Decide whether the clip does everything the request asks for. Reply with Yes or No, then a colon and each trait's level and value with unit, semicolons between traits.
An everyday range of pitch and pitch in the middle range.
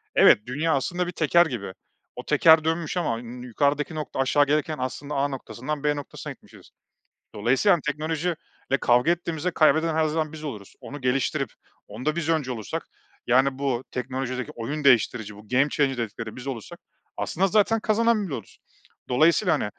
Yes: average, 4.2 semitones; medium, 145 Hz